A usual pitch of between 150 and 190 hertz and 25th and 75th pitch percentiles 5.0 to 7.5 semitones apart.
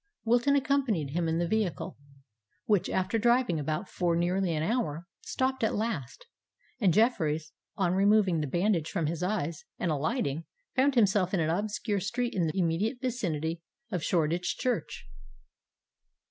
Yes: medium, 185 Hz; wide, 5.6 semitones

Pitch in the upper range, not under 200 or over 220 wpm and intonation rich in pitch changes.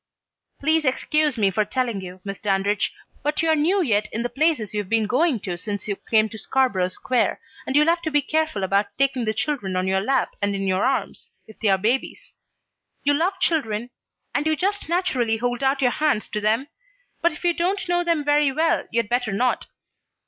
Yes: very high, 250 Hz; fast, 205 wpm; wide, 6.6 semitones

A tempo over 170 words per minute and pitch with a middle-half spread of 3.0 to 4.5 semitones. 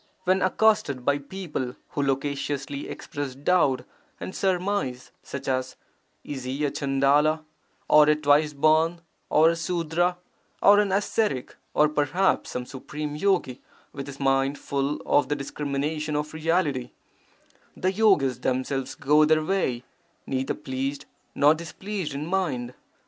No: slow, 135 wpm; average, 3.6 semitones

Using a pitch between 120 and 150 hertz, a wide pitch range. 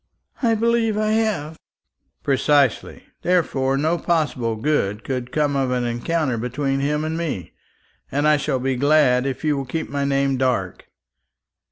No: medium, 140 Hz; average, 3.6 semitones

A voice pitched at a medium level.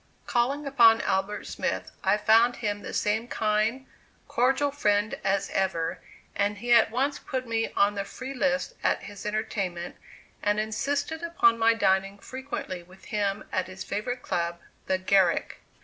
No: high, 215 Hz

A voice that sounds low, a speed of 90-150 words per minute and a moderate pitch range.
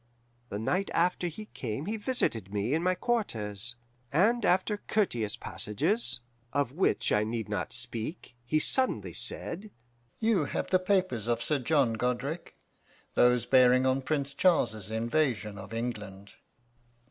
No: low, 130 Hz; average, 140 wpm; wide, 8.1 semitones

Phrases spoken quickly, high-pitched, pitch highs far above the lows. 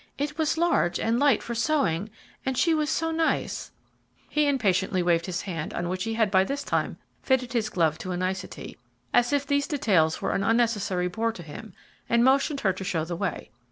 Yes: fast, 210 wpm; high, 225 Hz; wide, 7.2 semitones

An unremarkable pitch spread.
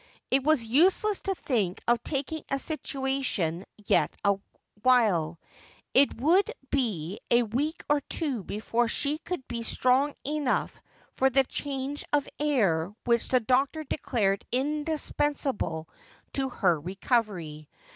No: wide, 5.9 semitones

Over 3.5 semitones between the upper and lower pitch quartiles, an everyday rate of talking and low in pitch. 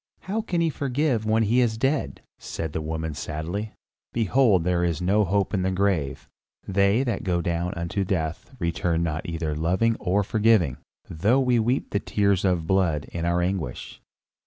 Yes: average, 4.9 semitones; average, 175 wpm; very low, 95 Hz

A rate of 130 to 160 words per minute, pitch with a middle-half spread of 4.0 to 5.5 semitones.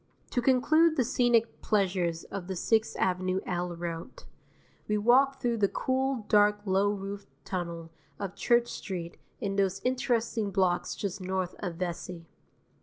Yes: average, 145 wpm; average, 4.6 semitones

